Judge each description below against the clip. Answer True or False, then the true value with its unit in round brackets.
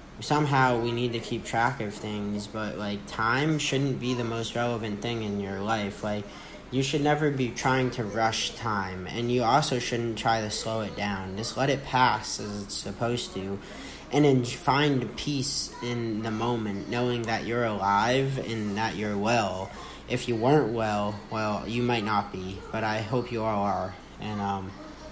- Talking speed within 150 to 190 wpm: True (185 wpm)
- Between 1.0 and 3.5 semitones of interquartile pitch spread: True (3.1 semitones)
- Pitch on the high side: False (115 Hz)